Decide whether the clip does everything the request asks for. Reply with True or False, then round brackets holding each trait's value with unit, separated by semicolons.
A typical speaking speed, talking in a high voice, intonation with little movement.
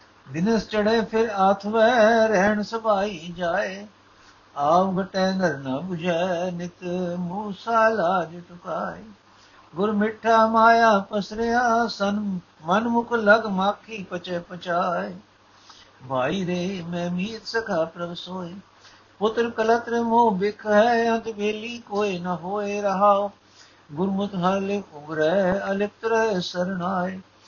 False (105 wpm; 195 Hz; 3.7 semitones)